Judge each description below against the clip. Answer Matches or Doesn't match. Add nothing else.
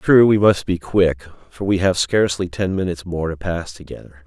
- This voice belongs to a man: Matches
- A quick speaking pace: Matches